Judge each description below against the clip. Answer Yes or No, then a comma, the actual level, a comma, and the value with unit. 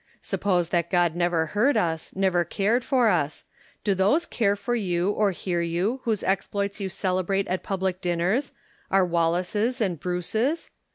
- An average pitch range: Yes, average, 3.2 semitones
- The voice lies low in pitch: No, high, 190 Hz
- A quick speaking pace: No, average, 170 wpm